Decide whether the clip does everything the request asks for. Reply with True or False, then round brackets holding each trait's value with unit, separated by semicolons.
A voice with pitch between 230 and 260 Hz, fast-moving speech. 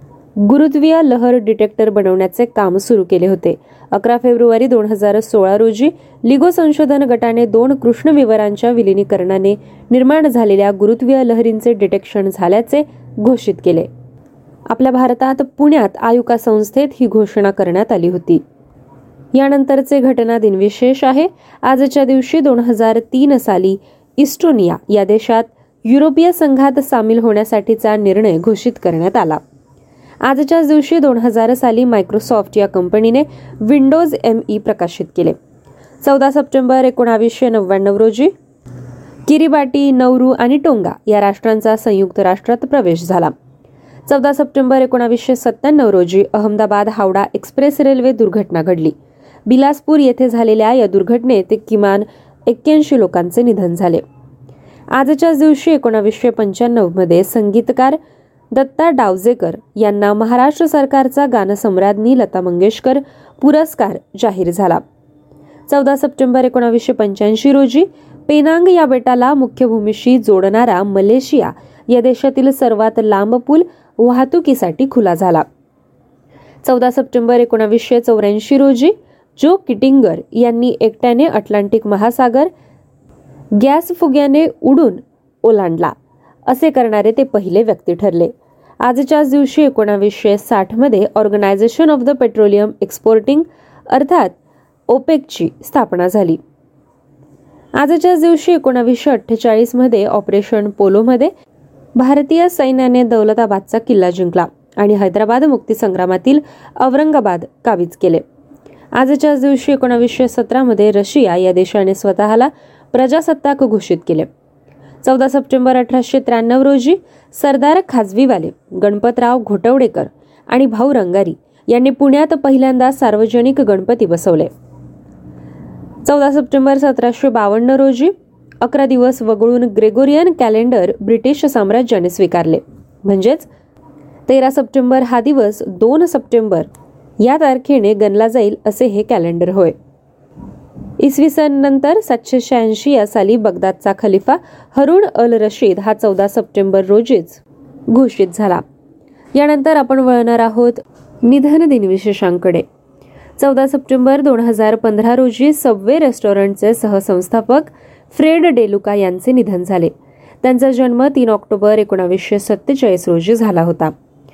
False (235 Hz; 110 wpm)